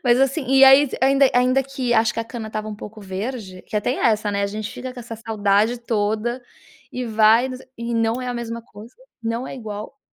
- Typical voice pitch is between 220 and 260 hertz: Yes, high, 230 Hz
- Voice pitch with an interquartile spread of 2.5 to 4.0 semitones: Yes, average, 2.8 semitones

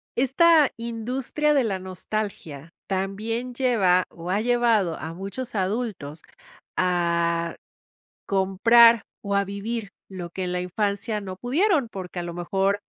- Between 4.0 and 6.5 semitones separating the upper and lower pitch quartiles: Yes, average, 4.5 semitones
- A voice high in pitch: Yes, high, 200 Hz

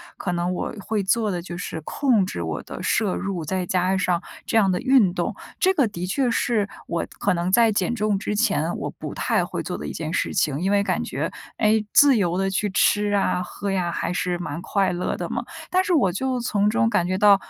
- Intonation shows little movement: No, average, 3.4 semitones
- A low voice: No, high, 195 Hz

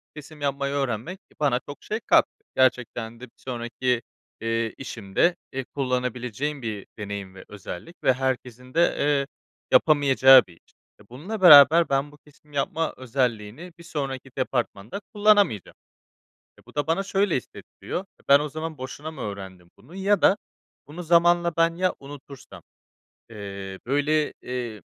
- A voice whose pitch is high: No, low, 135 Hz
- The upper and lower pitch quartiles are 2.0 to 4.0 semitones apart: No, average, 4.9 semitones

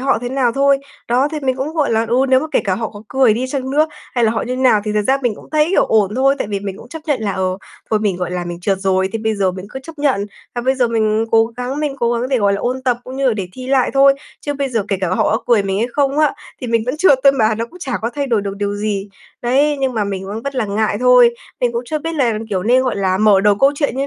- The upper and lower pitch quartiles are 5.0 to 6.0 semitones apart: No, average, 4.6 semitones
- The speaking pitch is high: Yes, high, 240 Hz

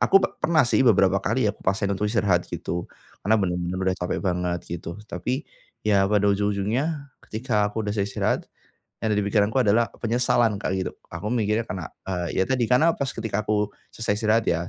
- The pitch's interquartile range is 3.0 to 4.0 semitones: Yes, average, 3.4 semitones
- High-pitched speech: No, low, 105 Hz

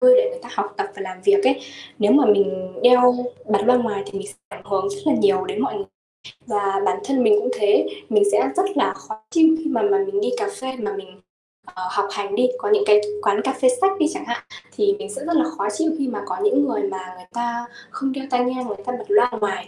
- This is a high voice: Yes, very high, 250 Hz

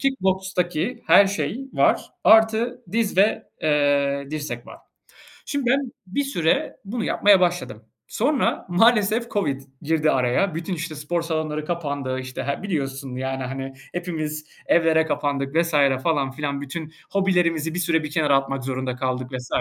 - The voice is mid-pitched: Yes, medium, 160 Hz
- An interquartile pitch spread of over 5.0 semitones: Yes, wide, 5.4 semitones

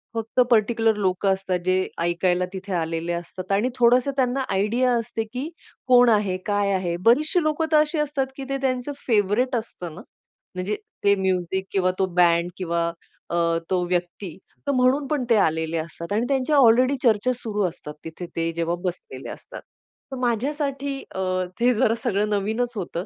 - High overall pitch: Yes, high, 210 Hz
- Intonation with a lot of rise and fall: Yes, wide, 5.7 semitones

